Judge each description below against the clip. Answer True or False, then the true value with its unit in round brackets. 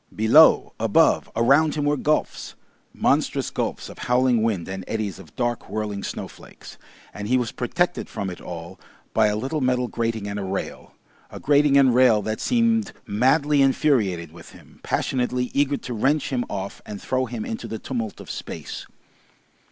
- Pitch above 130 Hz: False (120 Hz)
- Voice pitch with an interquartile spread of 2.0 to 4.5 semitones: False (5.0 semitones)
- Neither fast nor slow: True (170 wpm)